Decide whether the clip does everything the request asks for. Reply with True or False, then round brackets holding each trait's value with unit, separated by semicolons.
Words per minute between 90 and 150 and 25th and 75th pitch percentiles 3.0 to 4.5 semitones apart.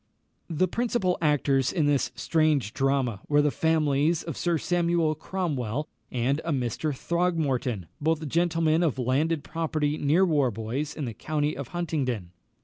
True (140 wpm; 3.5 semitones)